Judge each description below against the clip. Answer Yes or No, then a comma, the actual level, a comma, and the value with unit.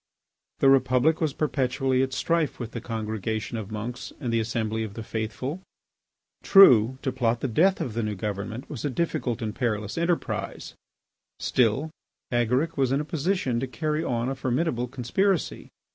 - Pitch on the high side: No, low, 125 Hz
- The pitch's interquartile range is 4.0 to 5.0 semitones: Yes, average, 4.5 semitones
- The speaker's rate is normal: Yes, average, 165 wpm